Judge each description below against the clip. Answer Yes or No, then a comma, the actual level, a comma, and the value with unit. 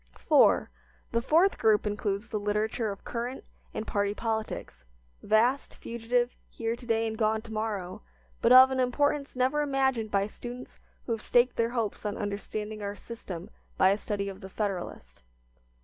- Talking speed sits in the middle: Yes, average, 165 wpm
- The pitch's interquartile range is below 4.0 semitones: Yes, average, 2.8 semitones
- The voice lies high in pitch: Yes, high, 220 Hz